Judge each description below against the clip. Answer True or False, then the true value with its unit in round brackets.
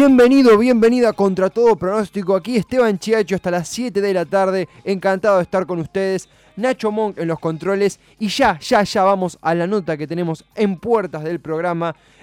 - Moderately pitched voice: False (195 Hz)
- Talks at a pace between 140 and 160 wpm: False (185 wpm)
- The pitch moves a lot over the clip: False (3.7 semitones)